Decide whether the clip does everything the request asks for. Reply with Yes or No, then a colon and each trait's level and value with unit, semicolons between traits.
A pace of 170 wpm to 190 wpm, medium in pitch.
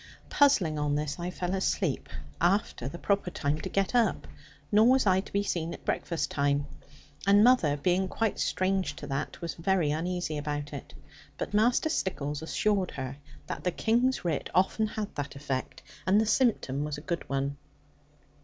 Yes: average, 175 wpm; medium, 175 Hz